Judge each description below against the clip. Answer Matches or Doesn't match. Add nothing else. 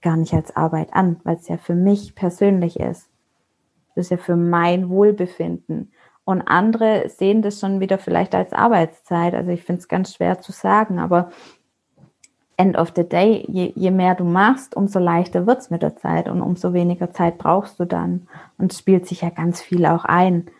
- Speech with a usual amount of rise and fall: Doesn't match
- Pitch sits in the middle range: Matches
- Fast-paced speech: Matches